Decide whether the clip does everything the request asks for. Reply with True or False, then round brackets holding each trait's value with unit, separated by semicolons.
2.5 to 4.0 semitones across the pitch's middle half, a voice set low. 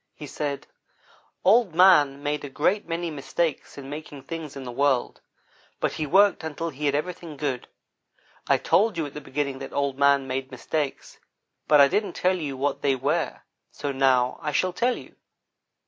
False (3.4 semitones; 145 Hz)